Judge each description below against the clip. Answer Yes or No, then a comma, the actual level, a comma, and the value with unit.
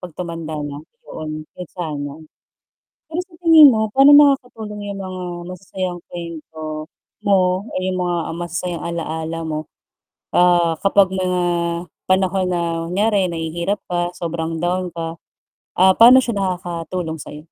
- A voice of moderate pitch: Yes, medium, 180 Hz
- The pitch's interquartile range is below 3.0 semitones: Yes, narrow, 2.6 semitones